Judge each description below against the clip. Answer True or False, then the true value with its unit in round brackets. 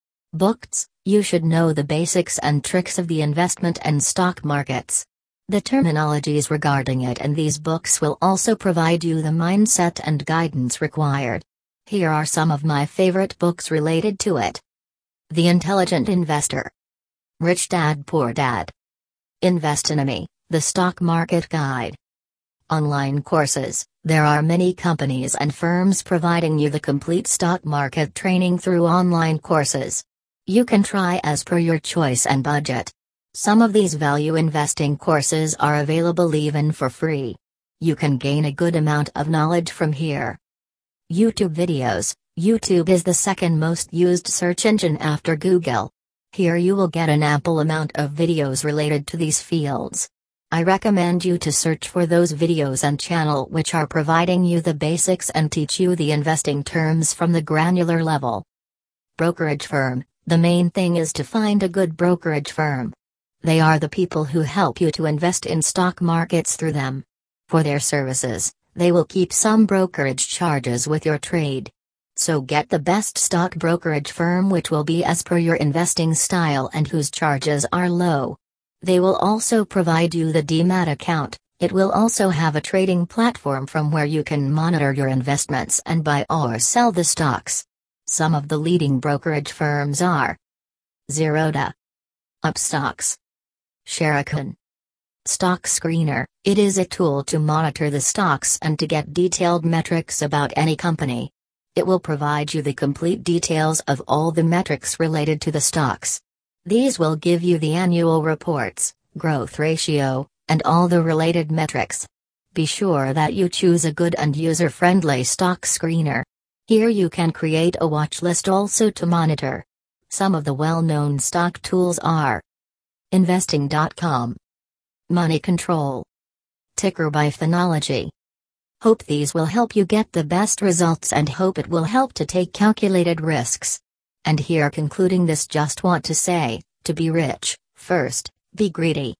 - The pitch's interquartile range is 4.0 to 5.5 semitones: False (3.2 semitones)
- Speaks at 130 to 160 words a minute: True (155 wpm)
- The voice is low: False (160 Hz)